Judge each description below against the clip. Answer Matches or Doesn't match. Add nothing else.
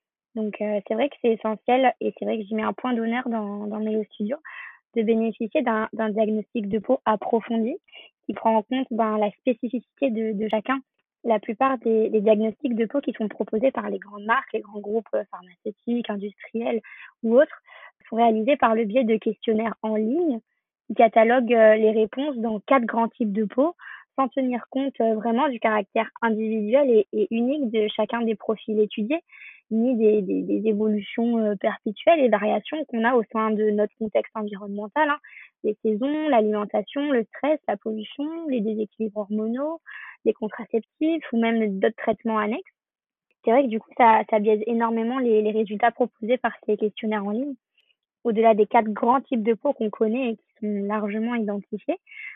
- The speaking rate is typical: Matches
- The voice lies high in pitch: Matches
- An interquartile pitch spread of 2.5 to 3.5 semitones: Matches